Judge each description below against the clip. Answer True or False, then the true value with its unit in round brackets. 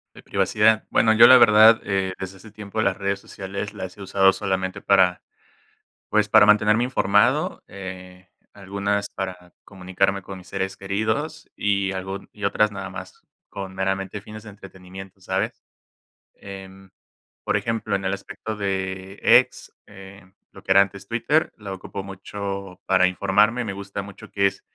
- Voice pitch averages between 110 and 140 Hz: False (100 Hz)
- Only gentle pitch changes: True (1.5 semitones)